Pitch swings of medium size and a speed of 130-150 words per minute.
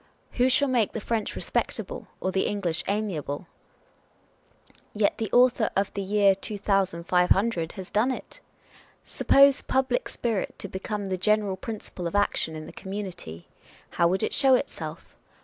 No: average, 3.2 semitones; average, 160 wpm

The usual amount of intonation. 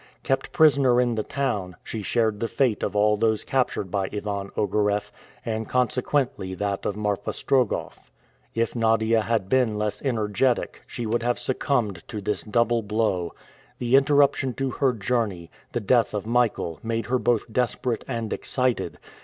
Yes: average, 3.2 semitones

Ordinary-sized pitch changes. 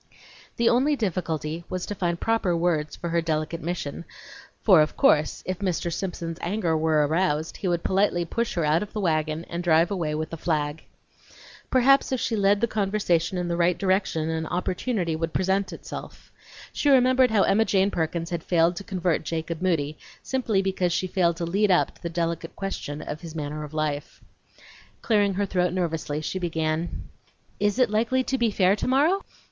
Yes: average, 3.7 semitones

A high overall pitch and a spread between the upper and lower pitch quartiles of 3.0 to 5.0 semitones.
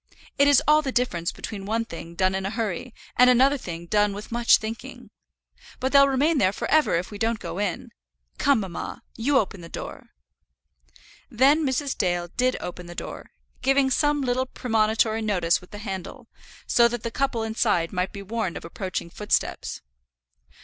No: high, 225 Hz; wide, 5.4 semitones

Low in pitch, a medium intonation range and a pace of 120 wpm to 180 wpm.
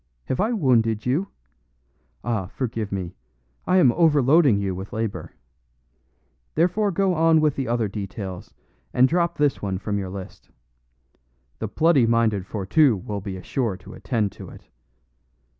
No: low, 115 Hz; wide, 7.5 semitones; average, 145 wpm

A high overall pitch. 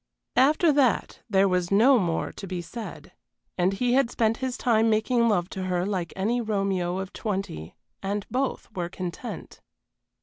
Yes: high, 200 Hz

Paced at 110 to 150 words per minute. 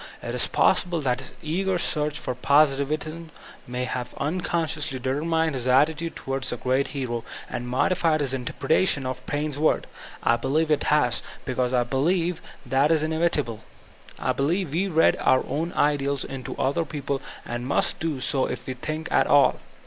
No: average, 170 wpm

